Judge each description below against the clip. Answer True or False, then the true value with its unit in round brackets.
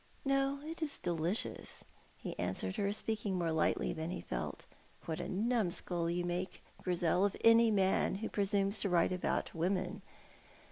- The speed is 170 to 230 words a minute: False (155 wpm)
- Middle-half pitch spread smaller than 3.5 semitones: False (4.0 semitones)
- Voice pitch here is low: False (185 Hz)